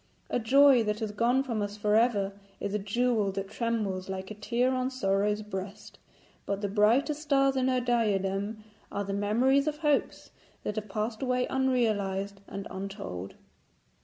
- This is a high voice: Yes, high, 215 Hz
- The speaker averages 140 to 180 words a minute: Yes, average, 165 wpm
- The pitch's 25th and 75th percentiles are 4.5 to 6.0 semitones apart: No, average, 4.0 semitones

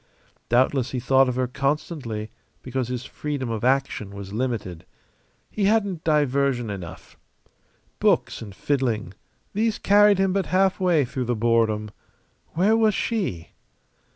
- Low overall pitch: Yes, low, 130 Hz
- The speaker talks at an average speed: No, slow, 130 wpm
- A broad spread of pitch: Yes, wide, 7.6 semitones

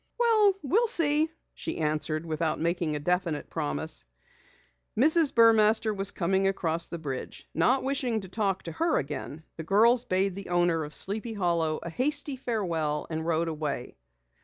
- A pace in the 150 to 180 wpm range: Yes, average, 155 wpm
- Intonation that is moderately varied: No, wide, 6.7 semitones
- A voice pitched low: No, medium, 185 Hz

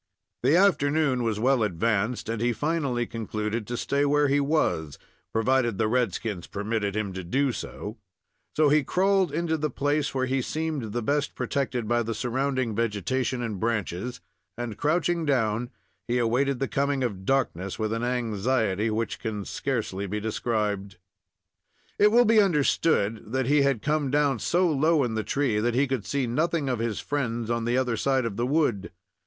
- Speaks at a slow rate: No, average, 180 wpm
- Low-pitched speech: Yes, low, 125 Hz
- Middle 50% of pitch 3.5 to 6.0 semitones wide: Yes, average, 4.4 semitones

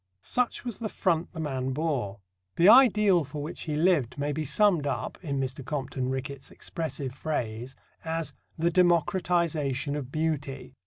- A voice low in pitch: No, medium, 150 Hz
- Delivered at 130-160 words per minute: Yes, average, 155 wpm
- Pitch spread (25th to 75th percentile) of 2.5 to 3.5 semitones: No, average, 4.1 semitones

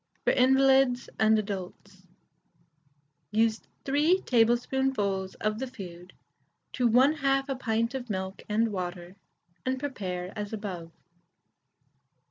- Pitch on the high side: Yes, high, 225 Hz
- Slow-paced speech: Yes, slow, 105 wpm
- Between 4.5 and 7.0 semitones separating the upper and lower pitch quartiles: Yes, wide, 5.5 semitones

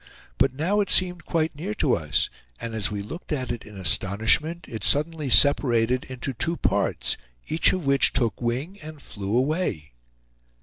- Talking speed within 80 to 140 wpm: No, average, 170 wpm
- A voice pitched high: No, low, 135 Hz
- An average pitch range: No, wide, 6.3 semitones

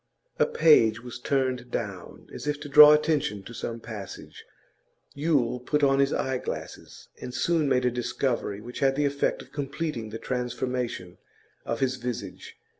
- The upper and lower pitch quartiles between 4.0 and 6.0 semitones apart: No, average, 3.3 semitones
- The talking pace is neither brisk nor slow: Yes, average, 160 wpm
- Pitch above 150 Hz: No, low, 125 Hz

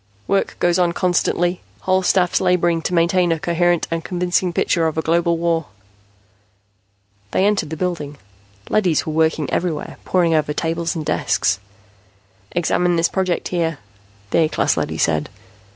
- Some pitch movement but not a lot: No, narrow, 1.7 semitones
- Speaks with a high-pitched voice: No, medium, 170 Hz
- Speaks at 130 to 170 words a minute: Yes, average, 150 wpm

